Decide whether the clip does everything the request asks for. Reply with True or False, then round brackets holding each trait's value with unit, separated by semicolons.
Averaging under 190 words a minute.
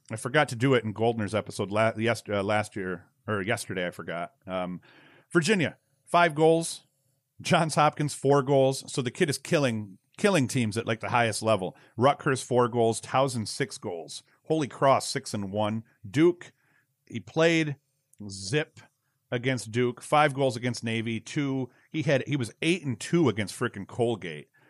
True (165 wpm)